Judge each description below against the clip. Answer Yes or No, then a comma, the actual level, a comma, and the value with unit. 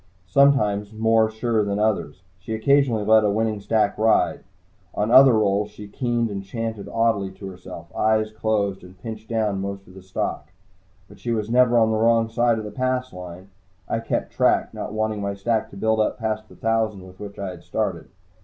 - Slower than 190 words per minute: No, average, 200 wpm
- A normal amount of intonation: No, narrow, 2.1 semitones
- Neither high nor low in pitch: No, low, 110 Hz